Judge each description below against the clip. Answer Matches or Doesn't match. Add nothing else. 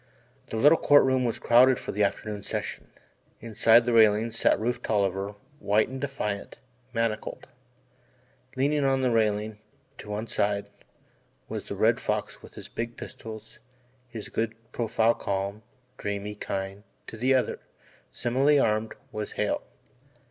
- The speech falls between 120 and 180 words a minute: Matches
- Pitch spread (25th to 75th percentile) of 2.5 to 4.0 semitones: Matches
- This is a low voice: Matches